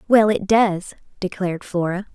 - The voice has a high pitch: Yes, high, 195 Hz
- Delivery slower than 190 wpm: Yes, average, 140 wpm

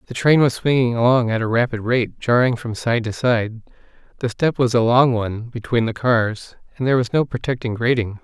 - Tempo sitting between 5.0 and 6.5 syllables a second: Yes, 5.4 syllables/s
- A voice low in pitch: Yes, low, 120 Hz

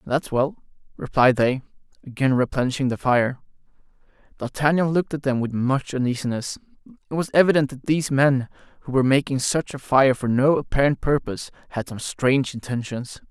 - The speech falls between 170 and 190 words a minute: No, average, 160 wpm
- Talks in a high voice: No, low, 135 Hz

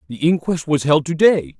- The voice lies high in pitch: No, medium, 150 Hz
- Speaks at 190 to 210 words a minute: No, fast, 225 wpm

